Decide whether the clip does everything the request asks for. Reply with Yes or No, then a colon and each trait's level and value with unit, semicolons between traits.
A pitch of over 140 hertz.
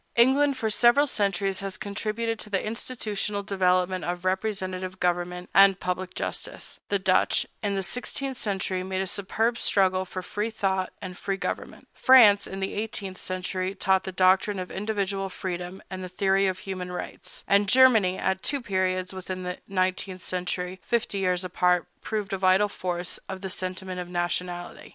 Yes: high, 190 Hz